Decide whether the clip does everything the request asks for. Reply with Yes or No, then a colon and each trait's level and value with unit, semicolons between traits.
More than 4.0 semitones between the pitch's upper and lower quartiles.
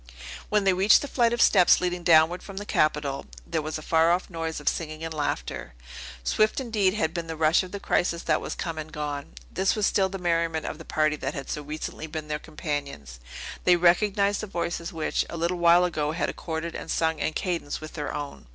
No: average, 2.9 semitones